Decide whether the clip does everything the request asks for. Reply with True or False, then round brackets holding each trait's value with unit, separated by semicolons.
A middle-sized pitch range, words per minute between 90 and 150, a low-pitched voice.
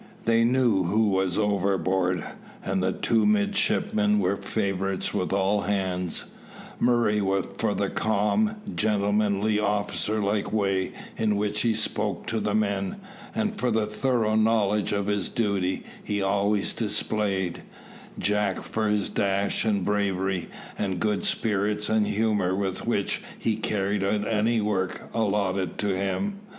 False (2.0 semitones; 140 wpm; 105 Hz)